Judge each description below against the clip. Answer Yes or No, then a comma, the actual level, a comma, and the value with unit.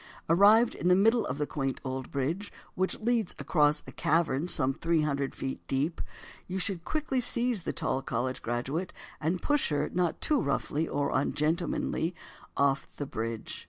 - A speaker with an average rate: Yes, average, 165 wpm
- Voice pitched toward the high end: No, medium, 160 Hz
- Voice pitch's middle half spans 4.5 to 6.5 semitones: Yes, wide, 5.5 semitones